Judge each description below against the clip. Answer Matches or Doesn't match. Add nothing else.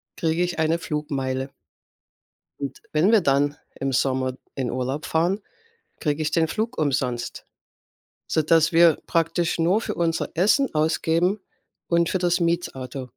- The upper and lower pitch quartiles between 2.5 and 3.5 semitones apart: Doesn't match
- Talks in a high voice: Doesn't match